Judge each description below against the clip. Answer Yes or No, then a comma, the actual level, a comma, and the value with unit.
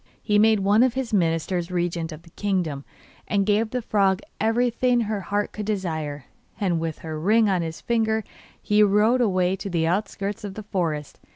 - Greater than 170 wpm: Yes, average, 185 wpm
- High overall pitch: Yes, high, 200 Hz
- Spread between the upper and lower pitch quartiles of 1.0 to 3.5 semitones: No, average, 4.1 semitones